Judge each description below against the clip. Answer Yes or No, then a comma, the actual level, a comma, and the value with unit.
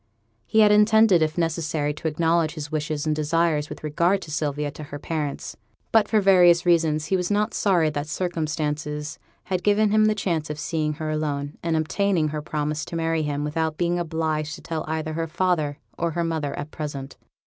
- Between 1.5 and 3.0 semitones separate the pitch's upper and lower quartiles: Yes, narrow, 2.4 semitones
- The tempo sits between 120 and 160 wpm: No, average, 195 wpm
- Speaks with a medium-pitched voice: Yes, medium, 160 Hz